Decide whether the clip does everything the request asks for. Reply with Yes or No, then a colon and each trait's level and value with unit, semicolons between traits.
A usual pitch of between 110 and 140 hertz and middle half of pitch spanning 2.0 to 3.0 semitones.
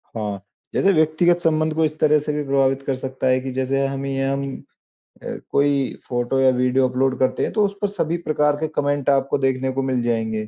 Yes: low, 135 Hz; average, 2.7 semitones